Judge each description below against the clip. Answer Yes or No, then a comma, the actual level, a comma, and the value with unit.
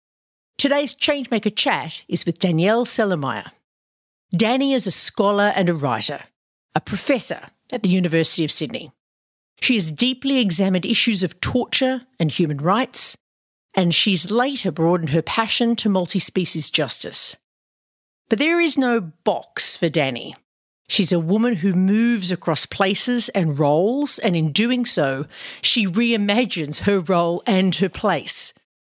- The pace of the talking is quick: No, average, 140 wpm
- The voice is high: Yes, high, 195 Hz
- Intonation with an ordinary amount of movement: No, wide, 6.0 semitones